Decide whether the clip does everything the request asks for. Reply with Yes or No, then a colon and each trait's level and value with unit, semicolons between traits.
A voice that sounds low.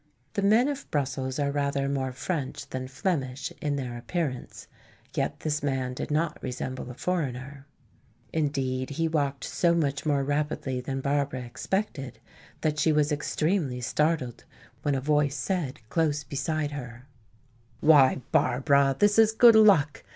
No: medium, 145 Hz